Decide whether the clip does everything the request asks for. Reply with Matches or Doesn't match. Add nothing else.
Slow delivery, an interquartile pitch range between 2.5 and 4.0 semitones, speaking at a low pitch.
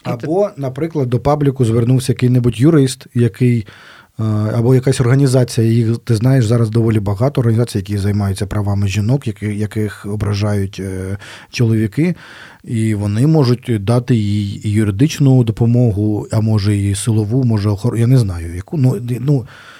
Doesn't match